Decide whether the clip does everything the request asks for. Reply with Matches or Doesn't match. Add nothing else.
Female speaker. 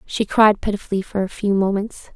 Matches